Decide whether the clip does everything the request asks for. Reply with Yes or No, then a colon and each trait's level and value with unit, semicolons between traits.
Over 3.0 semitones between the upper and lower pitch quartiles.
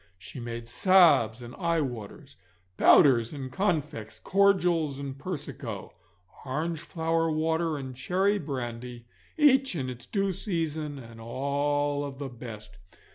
Yes: average, 5.3 semitones